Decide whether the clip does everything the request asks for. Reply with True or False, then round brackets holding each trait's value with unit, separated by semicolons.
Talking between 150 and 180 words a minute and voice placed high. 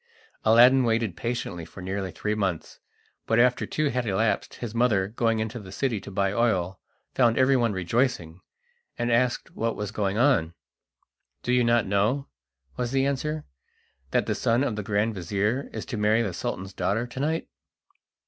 False (170 wpm; 115 Hz)